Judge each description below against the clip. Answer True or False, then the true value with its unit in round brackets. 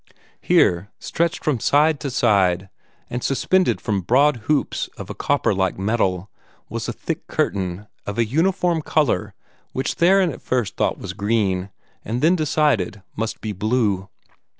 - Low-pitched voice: True (115 Hz)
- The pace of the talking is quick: False (150 wpm)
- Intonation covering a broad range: True (7.3 semitones)